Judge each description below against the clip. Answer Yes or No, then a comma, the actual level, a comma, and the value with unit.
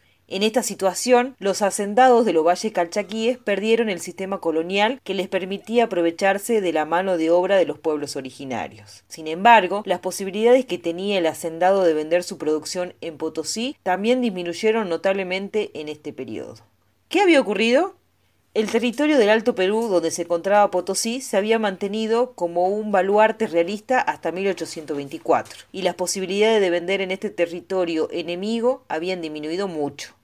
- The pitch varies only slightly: No, average, 4.5 semitones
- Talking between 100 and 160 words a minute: Yes, average, 155 wpm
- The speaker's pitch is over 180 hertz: Yes, high, 190 Hz